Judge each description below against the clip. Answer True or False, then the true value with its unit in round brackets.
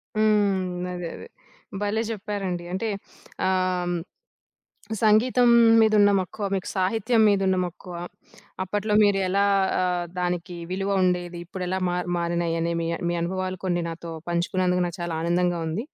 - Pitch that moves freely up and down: False (2.4 semitones)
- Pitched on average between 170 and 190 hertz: True (185 Hz)